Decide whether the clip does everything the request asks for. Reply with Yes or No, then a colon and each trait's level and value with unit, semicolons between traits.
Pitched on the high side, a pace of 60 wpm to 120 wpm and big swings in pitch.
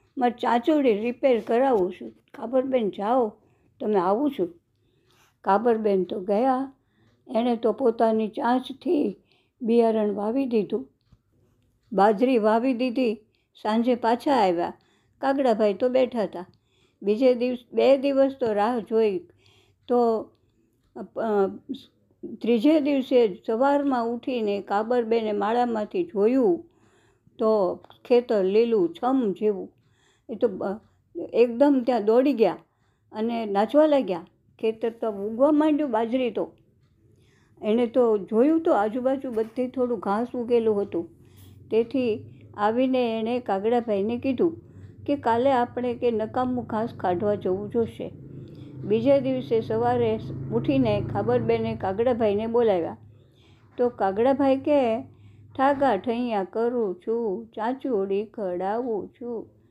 No: high, 225 Hz; average, 110 wpm; average, 4.1 semitones